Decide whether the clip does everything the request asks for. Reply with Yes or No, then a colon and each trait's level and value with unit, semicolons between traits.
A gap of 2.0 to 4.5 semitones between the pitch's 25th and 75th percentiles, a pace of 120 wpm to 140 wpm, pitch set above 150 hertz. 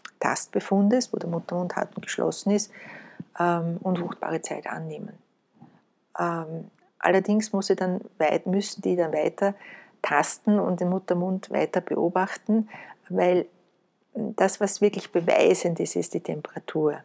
Yes: average, 2.8 semitones; average, 130 wpm; high, 190 Hz